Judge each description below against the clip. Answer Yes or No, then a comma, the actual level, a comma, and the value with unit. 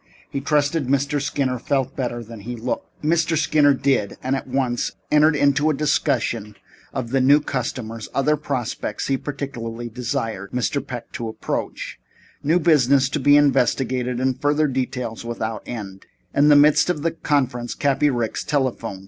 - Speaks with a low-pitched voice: Yes, low, 130 Hz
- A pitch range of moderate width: Yes, average, 3.2 semitones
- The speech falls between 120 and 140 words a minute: No, average, 165 wpm